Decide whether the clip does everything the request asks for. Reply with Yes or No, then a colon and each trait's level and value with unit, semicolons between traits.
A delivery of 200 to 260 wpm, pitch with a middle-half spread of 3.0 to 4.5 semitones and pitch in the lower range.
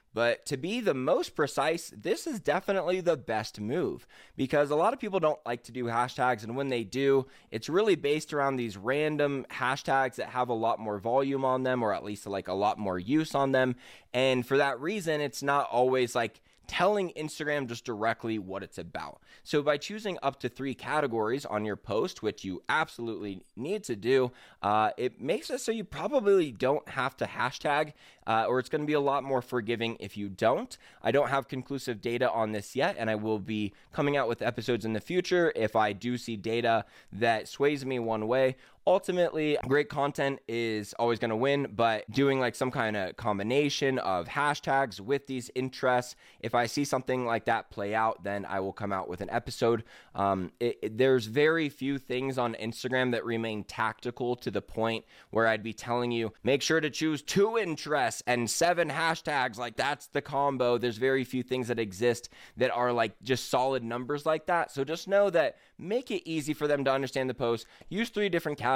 Yes: fast, 205 wpm; average, 4.2 semitones; low, 130 Hz